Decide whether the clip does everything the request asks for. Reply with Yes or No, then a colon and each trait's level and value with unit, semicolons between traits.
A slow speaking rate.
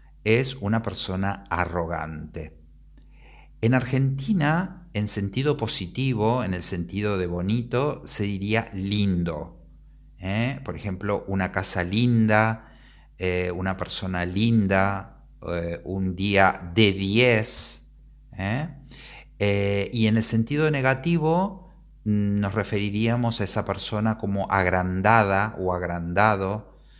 Yes: slow, 105 wpm